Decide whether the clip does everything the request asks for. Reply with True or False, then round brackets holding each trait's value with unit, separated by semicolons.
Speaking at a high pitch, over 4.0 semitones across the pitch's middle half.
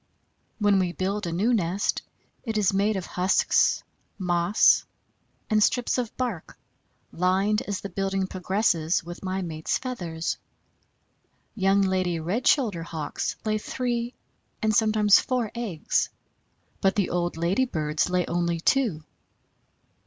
False (195 Hz; 3.7 semitones)